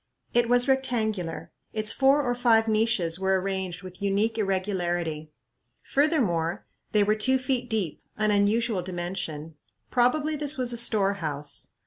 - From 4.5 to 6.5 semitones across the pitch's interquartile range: Yes, average, 5.2 semitones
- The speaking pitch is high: Yes, high, 210 Hz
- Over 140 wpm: No, slow, 135 wpm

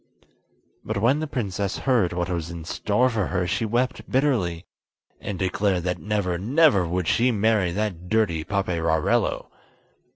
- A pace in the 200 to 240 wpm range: No, average, 150 wpm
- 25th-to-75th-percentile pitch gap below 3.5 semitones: No, average, 4.3 semitones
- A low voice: Yes, low, 100 Hz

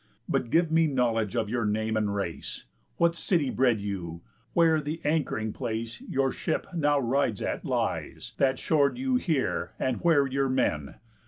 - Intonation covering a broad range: Yes, wide, 5.9 semitones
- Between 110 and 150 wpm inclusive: No, average, 165 wpm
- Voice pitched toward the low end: Yes, low, 130 Hz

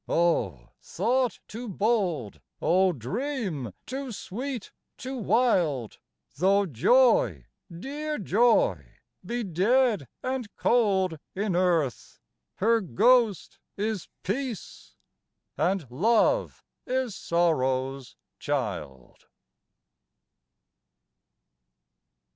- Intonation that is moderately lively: No, wide, 7.2 semitones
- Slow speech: Yes, slow, 80 wpm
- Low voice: No, high, 195 Hz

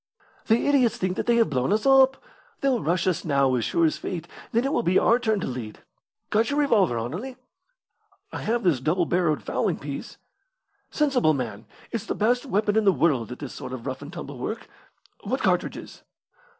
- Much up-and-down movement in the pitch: Yes, wide, 8.8 semitones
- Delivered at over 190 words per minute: Yes, average, 200 wpm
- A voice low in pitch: No, medium, 185 Hz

